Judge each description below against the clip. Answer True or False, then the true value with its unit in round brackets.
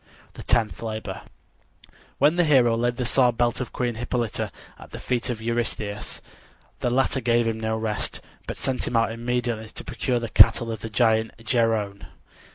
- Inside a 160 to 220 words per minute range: True (175 wpm)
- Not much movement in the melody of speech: True (1.7 semitones)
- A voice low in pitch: True (115 Hz)